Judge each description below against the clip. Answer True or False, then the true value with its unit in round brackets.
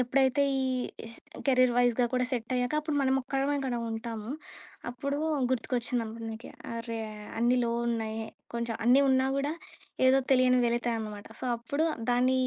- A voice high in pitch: True (245 Hz)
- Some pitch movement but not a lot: False (2.2 semitones)